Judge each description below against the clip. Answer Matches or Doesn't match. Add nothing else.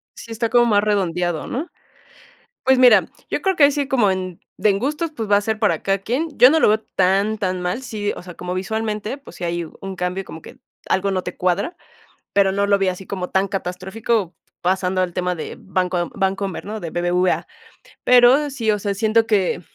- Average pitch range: Matches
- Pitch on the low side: Doesn't match